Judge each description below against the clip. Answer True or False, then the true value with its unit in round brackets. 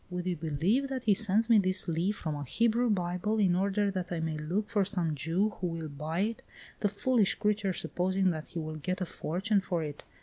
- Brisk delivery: True (225 wpm)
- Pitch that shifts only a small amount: False (4.1 semitones)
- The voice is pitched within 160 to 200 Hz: True (185 Hz)